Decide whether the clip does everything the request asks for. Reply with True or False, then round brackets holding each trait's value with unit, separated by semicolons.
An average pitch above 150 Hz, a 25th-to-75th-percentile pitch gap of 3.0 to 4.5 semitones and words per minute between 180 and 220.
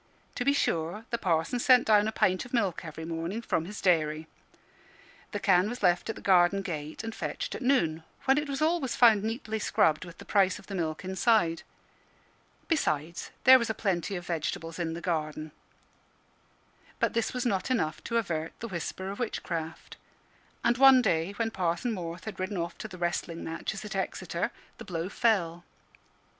False (190 Hz; 5.4 semitones; 185 wpm)